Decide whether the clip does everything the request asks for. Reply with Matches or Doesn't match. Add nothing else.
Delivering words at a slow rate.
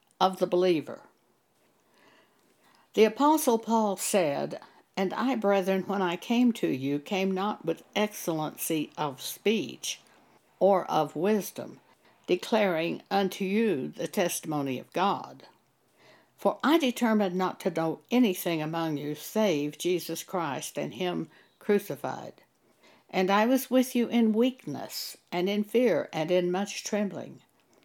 Matches